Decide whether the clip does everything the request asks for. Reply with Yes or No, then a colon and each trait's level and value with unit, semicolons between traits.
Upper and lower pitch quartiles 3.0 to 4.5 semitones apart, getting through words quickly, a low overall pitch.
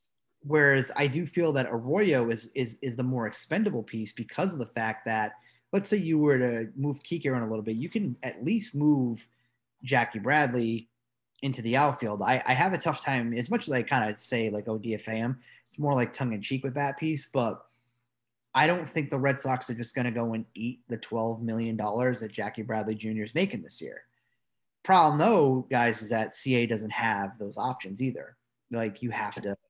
Yes: average, 3.5 semitones; fast, 210 wpm; low, 120 Hz